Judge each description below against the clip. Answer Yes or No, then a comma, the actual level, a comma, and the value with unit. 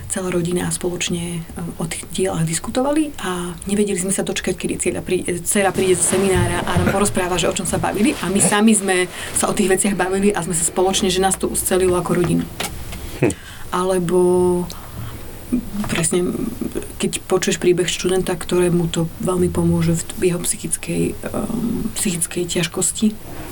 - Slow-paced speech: No, average, 160 wpm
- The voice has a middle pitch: Yes, medium, 180 Hz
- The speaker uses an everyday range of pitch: No, narrow, 1.7 semitones